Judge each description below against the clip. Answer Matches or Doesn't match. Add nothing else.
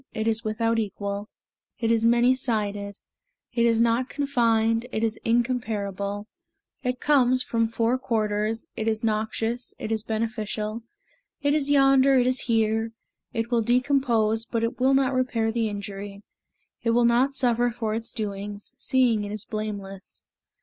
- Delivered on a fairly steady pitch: Matches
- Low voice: Doesn't match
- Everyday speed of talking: Matches